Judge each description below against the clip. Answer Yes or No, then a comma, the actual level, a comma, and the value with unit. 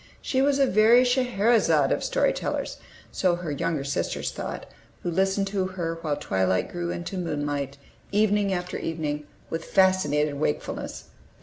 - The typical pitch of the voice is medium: Yes, medium, 175 Hz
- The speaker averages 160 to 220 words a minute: No, average, 145 wpm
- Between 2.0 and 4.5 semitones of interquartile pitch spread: No, average, 5.2 semitones